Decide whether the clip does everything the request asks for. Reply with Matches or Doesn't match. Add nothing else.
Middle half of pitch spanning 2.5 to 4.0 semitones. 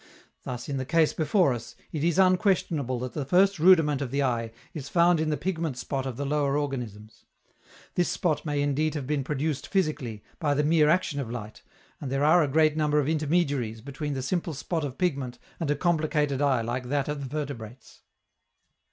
Matches